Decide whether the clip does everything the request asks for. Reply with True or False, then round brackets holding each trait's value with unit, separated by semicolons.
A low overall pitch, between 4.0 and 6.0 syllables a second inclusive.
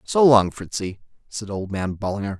True (105 Hz; 5.0 syllables/s)